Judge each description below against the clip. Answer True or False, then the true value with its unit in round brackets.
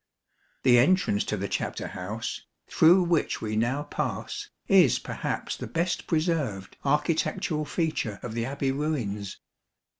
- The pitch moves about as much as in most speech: False (6.6 semitones)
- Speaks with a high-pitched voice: False (140 Hz)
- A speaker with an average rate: False (130 wpm)